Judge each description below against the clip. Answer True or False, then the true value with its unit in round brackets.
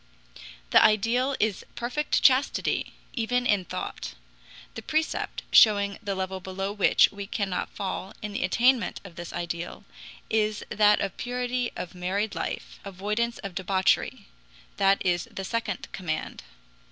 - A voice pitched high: True (205 Hz)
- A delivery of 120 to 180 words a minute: True (140 wpm)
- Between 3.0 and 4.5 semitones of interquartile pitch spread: True (3.6 semitones)